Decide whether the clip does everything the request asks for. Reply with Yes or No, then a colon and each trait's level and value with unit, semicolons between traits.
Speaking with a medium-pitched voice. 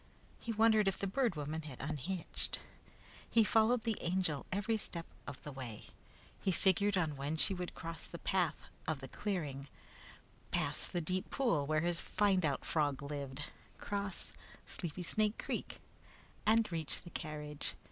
Yes: medium, 170 Hz